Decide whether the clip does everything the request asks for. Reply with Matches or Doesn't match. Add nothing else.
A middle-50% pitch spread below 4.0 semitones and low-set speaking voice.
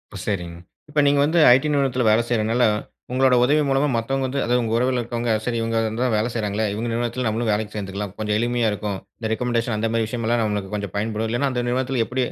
Matches